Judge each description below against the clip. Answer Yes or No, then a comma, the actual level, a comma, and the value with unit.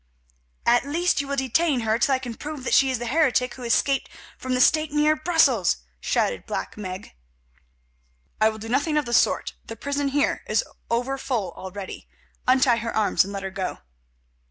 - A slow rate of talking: No, average, 190 wpm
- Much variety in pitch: No, average, 4.3 semitones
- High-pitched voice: Yes, very high, 255 Hz